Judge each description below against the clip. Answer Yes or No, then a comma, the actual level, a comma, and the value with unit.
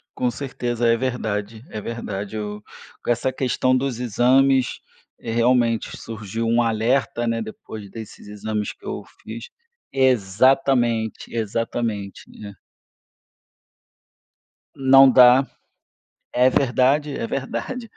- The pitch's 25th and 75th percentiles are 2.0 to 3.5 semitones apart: Yes, average, 2.8 semitones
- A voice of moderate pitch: No, low, 120 Hz